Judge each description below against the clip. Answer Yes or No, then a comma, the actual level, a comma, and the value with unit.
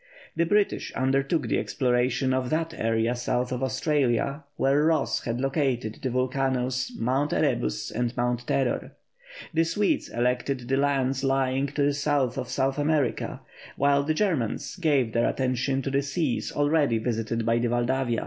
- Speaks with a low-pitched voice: Yes, low, 130 Hz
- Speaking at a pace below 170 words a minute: Yes, average, 160 wpm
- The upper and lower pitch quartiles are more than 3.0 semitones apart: No, average, 2.7 semitones